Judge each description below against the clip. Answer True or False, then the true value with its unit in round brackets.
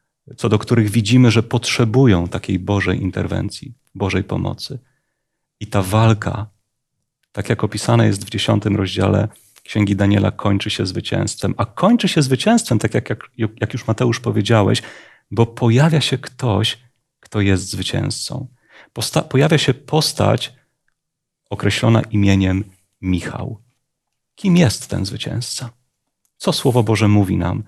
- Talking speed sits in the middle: True (125 wpm)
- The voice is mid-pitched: False (115 Hz)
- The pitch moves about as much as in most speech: True (3.9 semitones)